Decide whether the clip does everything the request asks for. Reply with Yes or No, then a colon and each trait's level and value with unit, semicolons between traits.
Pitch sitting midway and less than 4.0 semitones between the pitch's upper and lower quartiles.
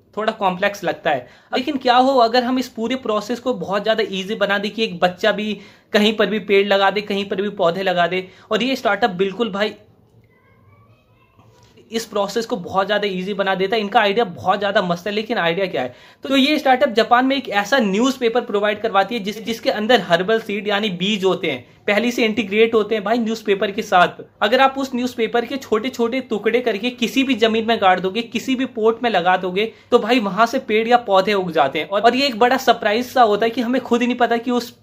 No: high, 220 Hz; average, 3.3 semitones